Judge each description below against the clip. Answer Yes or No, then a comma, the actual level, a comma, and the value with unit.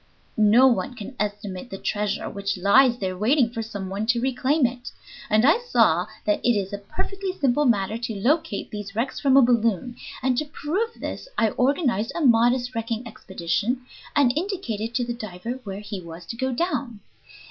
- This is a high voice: Yes, high, 235 Hz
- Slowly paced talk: No, average, 185 wpm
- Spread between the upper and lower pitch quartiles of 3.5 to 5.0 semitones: Yes, average, 4.2 semitones